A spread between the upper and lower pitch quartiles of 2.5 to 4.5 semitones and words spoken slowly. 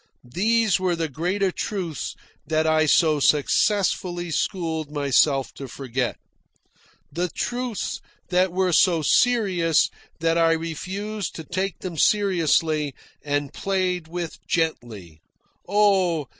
Yes: average, 3.5 semitones; slow, 115 wpm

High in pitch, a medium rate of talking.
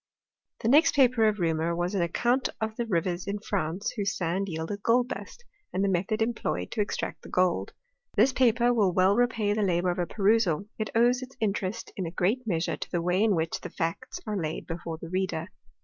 No: high, 195 Hz; fast, 210 wpm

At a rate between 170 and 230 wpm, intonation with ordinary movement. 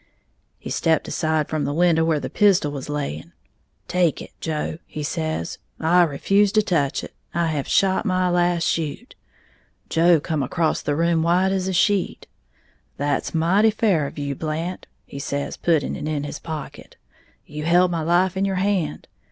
Yes: average, 175 wpm; average, 3.3 semitones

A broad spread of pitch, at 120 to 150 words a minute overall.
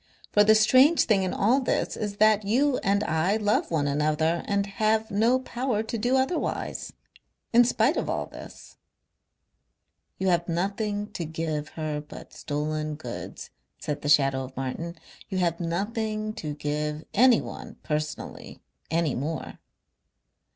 Yes: wide, 6.1 semitones; average, 145 wpm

